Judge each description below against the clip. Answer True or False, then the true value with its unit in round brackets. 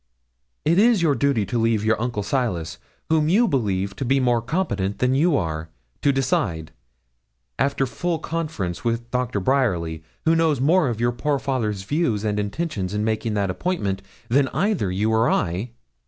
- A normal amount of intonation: False (5.9 semitones)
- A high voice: False (120 Hz)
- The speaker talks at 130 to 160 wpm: False (170 wpm)